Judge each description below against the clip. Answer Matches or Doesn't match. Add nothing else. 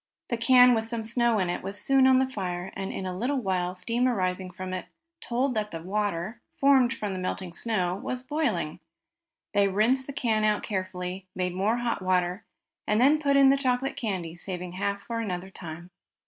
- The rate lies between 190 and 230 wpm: Matches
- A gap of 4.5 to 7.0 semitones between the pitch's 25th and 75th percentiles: Matches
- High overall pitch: Matches